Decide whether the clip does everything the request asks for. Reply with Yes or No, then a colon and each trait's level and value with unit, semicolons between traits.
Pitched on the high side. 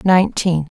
No: medium, 175 Hz